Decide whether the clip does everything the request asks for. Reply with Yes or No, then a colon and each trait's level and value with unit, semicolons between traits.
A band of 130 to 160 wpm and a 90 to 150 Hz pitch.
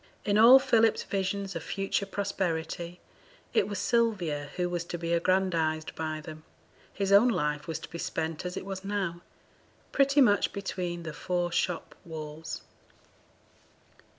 No: average, 150 wpm; medium, 180 Hz